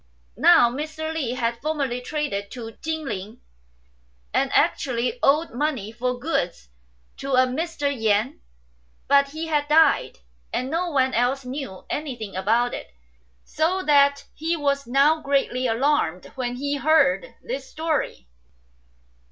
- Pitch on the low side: No, very high, 275 Hz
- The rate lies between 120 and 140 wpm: Yes, slow, 135 wpm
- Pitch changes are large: No, average, 4.1 semitones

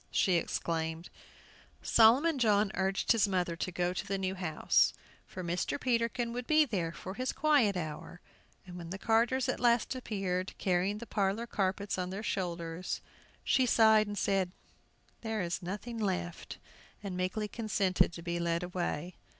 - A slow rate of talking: No, average, 160 wpm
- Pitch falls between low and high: No, high, 195 Hz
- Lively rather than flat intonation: No, average, 4.0 semitones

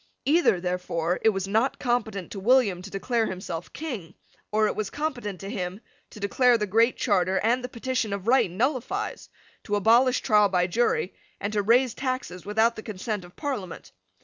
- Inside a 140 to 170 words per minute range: No, average, 180 wpm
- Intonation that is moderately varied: Yes, average, 4.6 semitones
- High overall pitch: Yes, high, 215 Hz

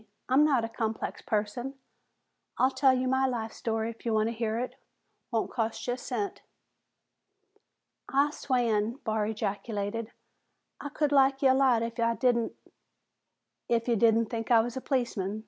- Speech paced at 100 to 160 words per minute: No, average, 170 wpm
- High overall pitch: Yes, high, 230 Hz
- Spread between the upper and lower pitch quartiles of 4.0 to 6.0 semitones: No, average, 2.7 semitones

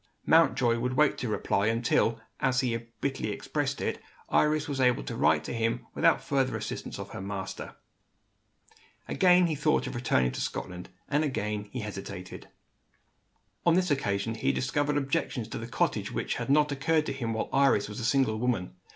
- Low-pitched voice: Yes, low, 125 Hz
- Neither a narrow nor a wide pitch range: Yes, average, 4.9 semitones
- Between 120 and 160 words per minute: No, average, 175 wpm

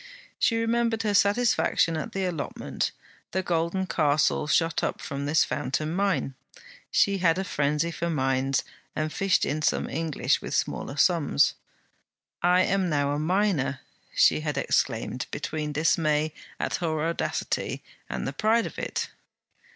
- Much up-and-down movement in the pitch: No, average, 4.2 semitones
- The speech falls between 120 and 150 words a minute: Yes, average, 145 wpm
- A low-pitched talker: No, medium, 165 Hz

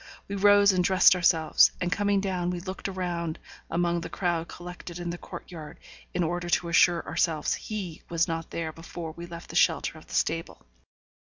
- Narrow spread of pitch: Yes, narrow, 1.6 semitones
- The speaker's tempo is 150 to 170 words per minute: No, average, 190 wpm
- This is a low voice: No, medium, 175 Hz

